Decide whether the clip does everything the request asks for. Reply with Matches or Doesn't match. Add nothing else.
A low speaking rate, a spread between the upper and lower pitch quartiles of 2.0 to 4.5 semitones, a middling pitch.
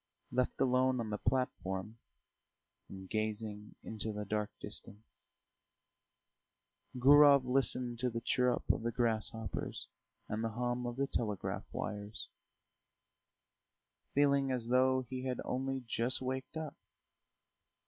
Doesn't match